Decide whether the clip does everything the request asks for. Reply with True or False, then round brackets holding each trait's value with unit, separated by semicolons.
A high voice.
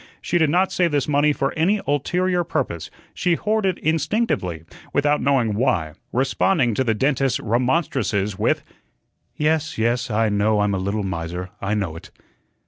False (130 Hz)